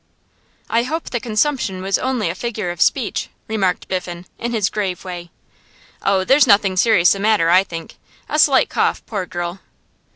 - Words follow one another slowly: No, average, 170 wpm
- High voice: Yes, high, 200 Hz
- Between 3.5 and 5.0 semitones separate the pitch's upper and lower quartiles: Yes, average, 4.4 semitones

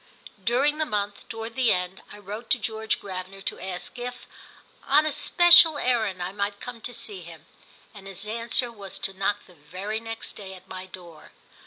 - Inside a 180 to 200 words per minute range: Yes, average, 190 wpm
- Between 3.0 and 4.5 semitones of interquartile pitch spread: Yes, average, 3.9 semitones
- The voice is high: Yes, high, 205 Hz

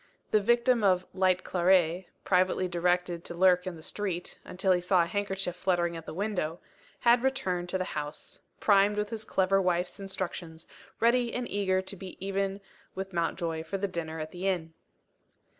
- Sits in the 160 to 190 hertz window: Yes, medium, 185 Hz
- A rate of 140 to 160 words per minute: No, average, 175 wpm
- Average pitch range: No, narrow, 2.2 semitones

